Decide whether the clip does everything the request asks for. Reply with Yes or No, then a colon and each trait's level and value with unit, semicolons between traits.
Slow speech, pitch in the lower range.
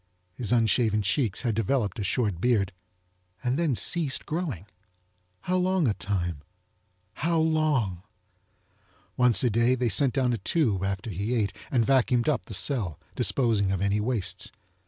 No: average, 155 wpm; low, 115 Hz